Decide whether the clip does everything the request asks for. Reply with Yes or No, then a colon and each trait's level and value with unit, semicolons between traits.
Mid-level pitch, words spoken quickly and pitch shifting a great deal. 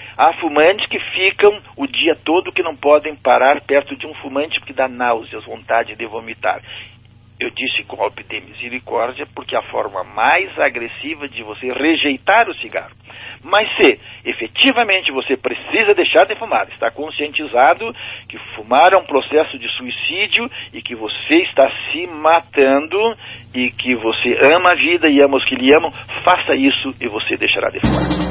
No: medium, 145 Hz; average, 165 wpm; wide, 6.1 semitones